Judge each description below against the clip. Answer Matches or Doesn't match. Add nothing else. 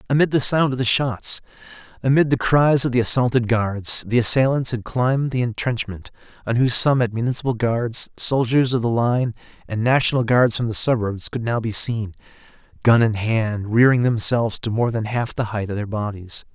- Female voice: Doesn't match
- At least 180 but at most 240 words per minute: Matches